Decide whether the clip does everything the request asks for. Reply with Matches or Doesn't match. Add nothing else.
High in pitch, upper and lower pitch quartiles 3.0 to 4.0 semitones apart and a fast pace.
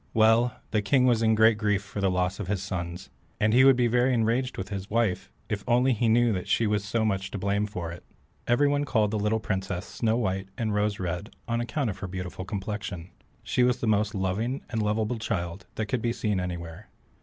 Doesn't match